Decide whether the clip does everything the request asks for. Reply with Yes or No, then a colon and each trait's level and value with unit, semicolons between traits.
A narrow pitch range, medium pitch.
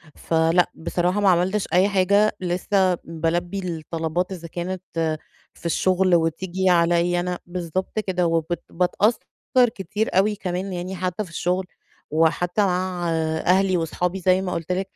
Yes: narrow, 1.7 semitones; medium, 180 Hz